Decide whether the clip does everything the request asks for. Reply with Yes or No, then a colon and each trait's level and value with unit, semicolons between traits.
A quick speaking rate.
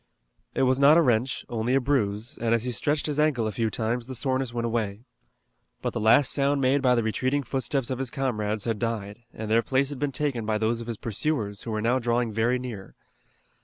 Yes: fast, 230 wpm